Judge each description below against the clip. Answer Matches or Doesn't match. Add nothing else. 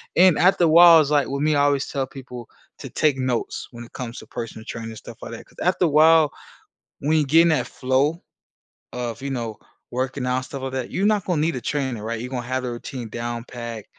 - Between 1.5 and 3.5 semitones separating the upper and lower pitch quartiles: Doesn't match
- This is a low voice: Matches